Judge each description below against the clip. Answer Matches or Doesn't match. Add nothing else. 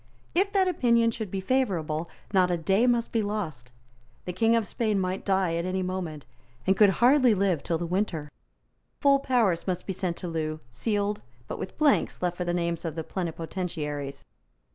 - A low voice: Doesn't match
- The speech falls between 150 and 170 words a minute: Doesn't match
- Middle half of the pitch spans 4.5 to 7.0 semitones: Matches